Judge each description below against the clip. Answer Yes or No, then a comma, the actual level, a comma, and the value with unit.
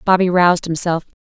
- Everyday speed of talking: Yes, average, 145 wpm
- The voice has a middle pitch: Yes, medium, 175 Hz